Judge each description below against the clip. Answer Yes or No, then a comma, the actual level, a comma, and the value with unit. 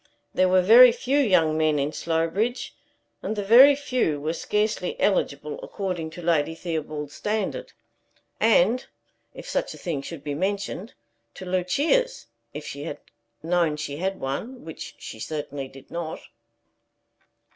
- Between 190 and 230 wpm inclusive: No, average, 145 wpm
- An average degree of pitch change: No, wide, 6.3 semitones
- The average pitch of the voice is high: No, medium, 180 Hz